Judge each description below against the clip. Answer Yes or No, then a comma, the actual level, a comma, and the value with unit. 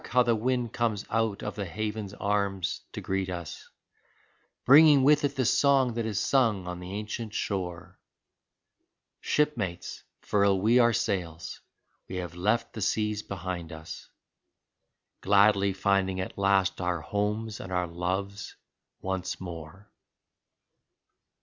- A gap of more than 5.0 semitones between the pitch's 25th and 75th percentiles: No, average, 3.5 semitones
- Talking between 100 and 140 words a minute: Yes, slow, 135 wpm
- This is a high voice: No, low, 100 Hz